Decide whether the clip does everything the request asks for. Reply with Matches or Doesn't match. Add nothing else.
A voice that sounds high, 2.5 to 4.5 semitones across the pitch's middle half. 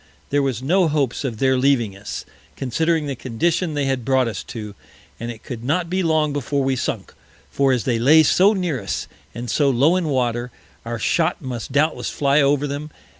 Doesn't match